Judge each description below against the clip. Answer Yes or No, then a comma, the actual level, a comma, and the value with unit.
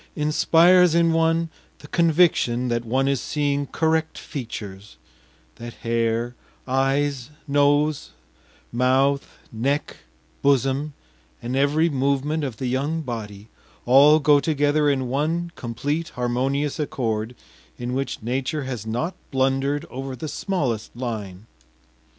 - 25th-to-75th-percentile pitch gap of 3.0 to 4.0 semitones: Yes, average, 3.6 semitones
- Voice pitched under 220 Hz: Yes, low, 135 Hz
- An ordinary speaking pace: No, slow, 115 wpm